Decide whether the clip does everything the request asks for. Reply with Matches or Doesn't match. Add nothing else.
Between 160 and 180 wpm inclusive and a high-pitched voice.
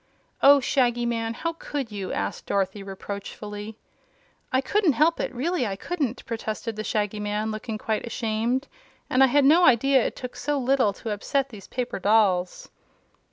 Matches